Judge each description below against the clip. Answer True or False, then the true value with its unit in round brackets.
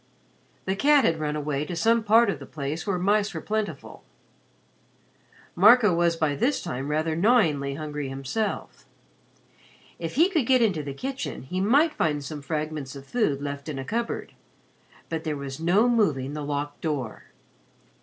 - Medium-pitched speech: True (160 Hz)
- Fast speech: False (165 wpm)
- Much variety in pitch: True (7.1 semitones)